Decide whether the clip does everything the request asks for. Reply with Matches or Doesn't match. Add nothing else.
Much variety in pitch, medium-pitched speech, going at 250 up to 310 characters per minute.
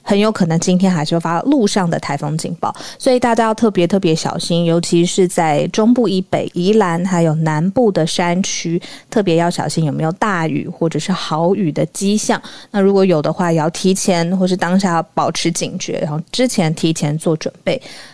Doesn't match